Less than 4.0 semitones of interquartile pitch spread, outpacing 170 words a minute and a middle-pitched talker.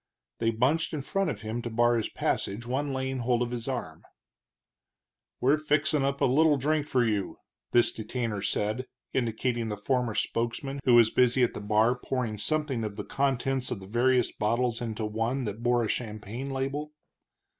No: average, 3.2 semitones; average, 180 wpm; low, 120 Hz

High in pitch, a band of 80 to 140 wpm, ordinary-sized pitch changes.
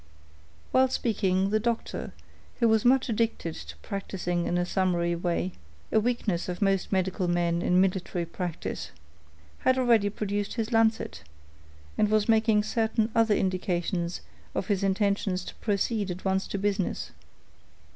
Yes: high, 195 Hz; slow, 135 wpm; average, 3.8 semitones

